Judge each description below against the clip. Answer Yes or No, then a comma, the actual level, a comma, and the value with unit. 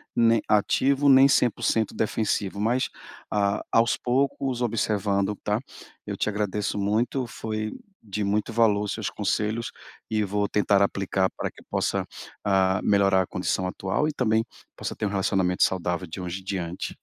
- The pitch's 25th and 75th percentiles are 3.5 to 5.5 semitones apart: No, average, 2.7 semitones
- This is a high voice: No, low, 105 Hz